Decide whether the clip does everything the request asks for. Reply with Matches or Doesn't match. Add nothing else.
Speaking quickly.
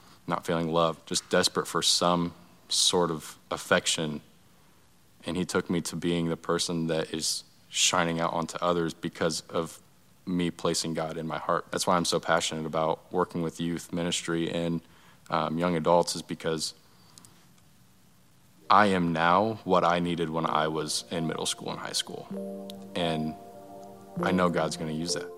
Doesn't match